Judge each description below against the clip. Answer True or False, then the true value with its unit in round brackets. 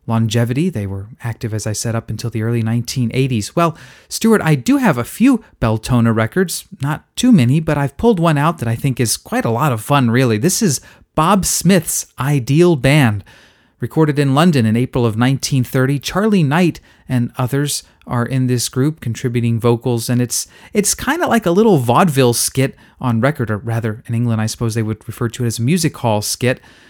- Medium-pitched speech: False (130 Hz)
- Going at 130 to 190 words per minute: False (205 wpm)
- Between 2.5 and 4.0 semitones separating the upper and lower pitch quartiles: False (5.0 semitones)